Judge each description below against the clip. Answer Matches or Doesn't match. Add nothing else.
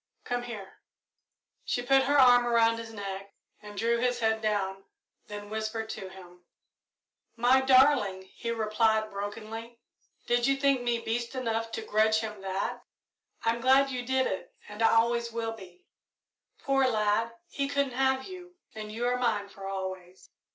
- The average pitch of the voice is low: Doesn't match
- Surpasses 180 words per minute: Doesn't match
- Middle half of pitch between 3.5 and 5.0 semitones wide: Doesn't match